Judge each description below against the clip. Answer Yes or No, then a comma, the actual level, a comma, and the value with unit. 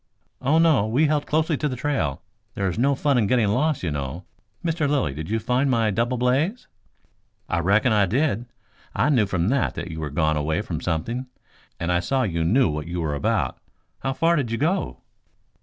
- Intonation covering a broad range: Yes, wide, 8.4 semitones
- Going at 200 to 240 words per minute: Yes, fast, 205 wpm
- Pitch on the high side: No, low, 115 Hz